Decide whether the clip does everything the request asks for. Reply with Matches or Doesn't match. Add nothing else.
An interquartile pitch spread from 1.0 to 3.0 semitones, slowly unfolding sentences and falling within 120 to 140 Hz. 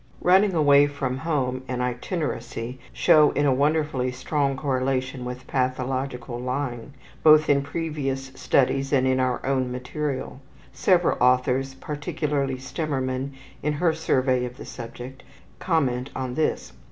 Matches